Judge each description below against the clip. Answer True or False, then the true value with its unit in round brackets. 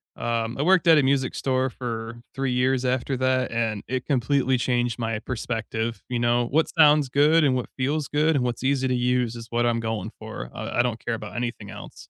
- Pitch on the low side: True (125 Hz)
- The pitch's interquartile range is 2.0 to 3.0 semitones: True (2.4 semitones)